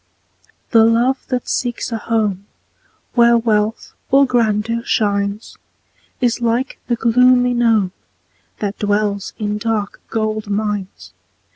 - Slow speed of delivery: Yes, slow, 115 wpm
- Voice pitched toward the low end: No, high, 225 Hz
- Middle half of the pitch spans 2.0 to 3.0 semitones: Yes, narrow, 2.4 semitones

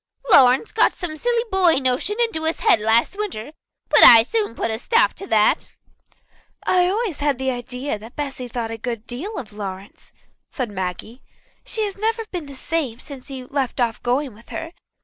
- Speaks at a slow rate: No, average, 190 wpm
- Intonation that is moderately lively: No, wide, 7.6 semitones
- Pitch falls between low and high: No, very high, 265 Hz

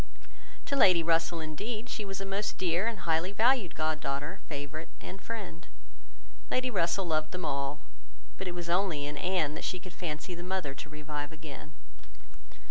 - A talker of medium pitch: Yes, medium, 170 Hz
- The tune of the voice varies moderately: Yes, average, 3.8 semitones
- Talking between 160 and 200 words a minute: Yes, average, 175 wpm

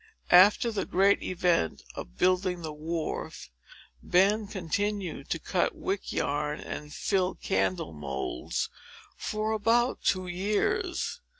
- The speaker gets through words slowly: Yes, slow, 115 wpm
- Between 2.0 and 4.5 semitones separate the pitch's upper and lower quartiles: No, average, 5.2 semitones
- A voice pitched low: No, medium, 185 Hz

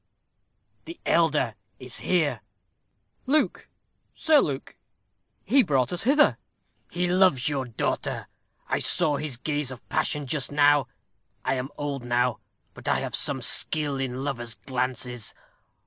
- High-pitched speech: No, medium, 145 Hz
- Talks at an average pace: No, slow, 130 wpm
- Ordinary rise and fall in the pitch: Yes, average, 4.3 semitones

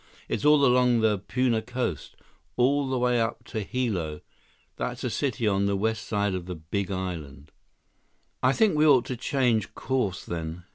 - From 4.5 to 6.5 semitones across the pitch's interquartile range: Yes, wide, 5.4 semitones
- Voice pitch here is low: Yes, low, 110 Hz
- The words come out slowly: No, average, 170 wpm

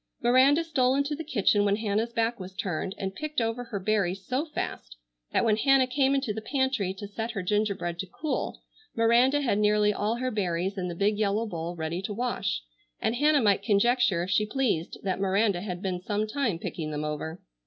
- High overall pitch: Yes, high, 210 Hz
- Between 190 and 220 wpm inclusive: Yes, fast, 205 wpm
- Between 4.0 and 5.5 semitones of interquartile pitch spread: Yes, average, 4.5 semitones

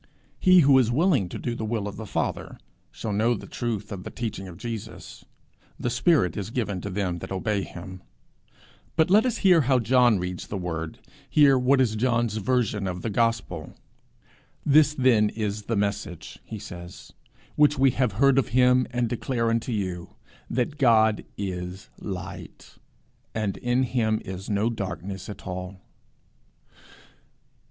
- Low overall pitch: Yes, low, 110 Hz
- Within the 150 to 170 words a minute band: Yes, average, 160 wpm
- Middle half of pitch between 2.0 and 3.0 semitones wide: No, average, 4.5 semitones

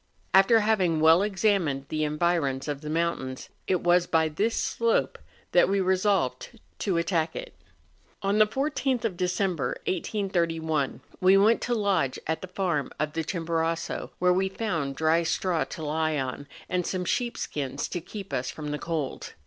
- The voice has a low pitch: No, medium, 170 Hz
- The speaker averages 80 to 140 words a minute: No, average, 170 wpm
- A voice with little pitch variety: No, average, 4.1 semitones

